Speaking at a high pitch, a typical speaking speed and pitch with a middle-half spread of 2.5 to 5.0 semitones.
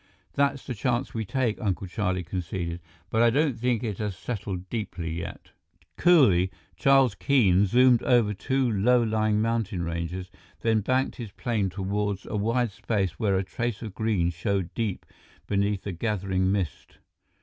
No: low, 105 Hz; average, 160 wpm; average, 4.0 semitones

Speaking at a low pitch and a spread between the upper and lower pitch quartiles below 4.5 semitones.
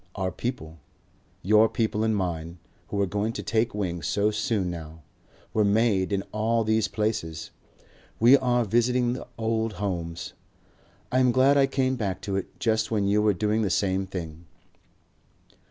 Yes: low, 105 Hz; average, 3.5 semitones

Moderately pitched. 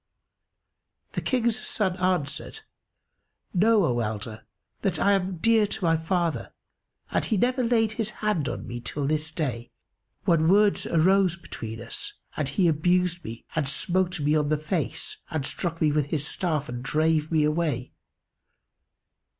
Yes: medium, 165 Hz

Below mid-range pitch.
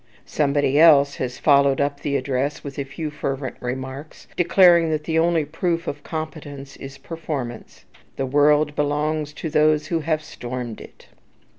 No: medium, 145 Hz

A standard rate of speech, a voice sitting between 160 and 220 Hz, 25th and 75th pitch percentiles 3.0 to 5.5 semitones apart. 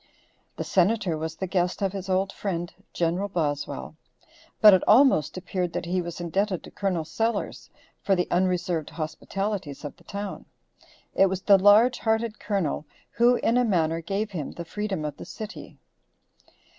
Yes: average, 165 wpm; medium, 185 Hz; average, 3.5 semitones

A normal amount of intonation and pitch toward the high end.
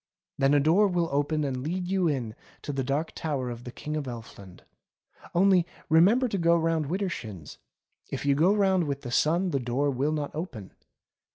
No: average, 4.6 semitones; medium, 150 Hz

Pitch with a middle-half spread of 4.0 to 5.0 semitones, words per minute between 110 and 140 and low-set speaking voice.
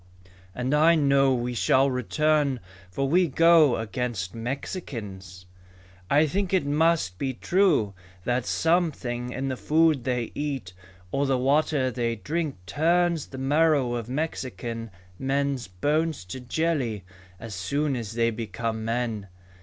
Yes: average, 4.7 semitones; slow, 135 wpm; low, 130 Hz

